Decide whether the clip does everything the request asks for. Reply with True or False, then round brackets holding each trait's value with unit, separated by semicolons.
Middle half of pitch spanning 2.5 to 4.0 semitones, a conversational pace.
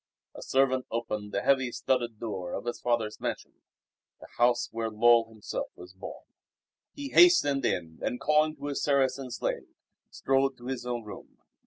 True (3.3 semitones; 165 wpm)